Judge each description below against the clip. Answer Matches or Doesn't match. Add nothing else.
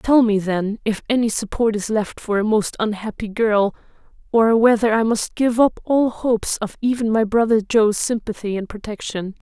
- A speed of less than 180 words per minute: Doesn't match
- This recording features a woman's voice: Matches